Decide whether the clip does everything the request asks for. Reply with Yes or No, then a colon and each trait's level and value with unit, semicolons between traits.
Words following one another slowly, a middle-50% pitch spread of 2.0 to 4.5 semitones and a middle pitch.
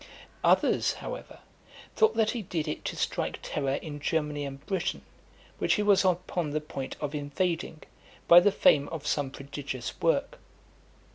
No: average, 155 wpm; average, 4.2 semitones; medium, 155 Hz